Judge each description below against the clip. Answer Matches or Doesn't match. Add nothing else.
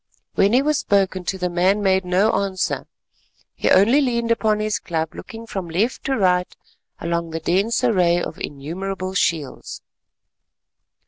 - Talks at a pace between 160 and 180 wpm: Doesn't match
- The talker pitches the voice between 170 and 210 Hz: Matches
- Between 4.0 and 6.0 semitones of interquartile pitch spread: Doesn't match